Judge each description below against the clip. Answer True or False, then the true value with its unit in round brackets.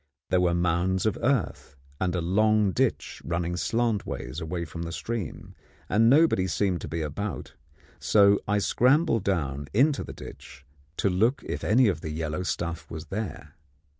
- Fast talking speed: False (165 wpm)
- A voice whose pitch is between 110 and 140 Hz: False (95 Hz)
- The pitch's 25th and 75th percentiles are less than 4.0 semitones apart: False (4.6 semitones)